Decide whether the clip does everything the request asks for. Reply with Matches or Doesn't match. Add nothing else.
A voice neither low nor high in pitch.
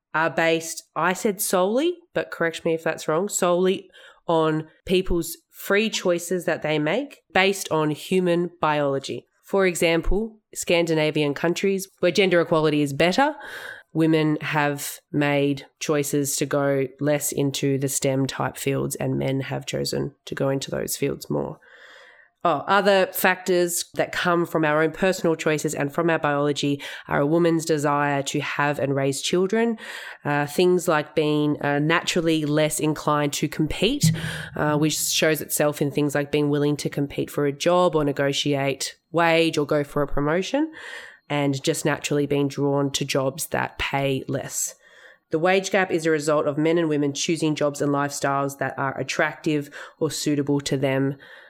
Matches